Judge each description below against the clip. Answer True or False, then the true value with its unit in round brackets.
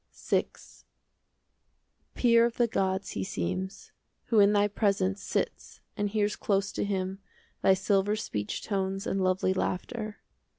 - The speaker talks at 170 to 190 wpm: False (135 wpm)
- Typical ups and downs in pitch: False (1.7 semitones)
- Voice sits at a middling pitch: False (195 Hz)